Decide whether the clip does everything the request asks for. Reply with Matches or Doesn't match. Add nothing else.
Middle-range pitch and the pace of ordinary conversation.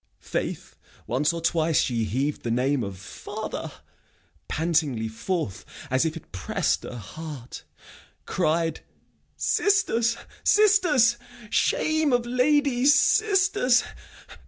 Doesn't match